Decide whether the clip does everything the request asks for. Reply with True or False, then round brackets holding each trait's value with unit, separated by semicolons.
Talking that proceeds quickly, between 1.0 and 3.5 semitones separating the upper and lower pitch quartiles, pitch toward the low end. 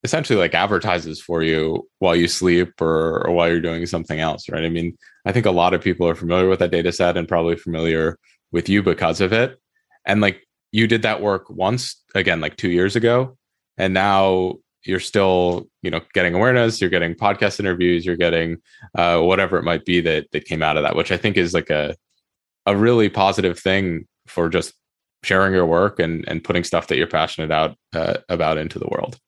True (210 wpm; 2.6 semitones; 90 Hz)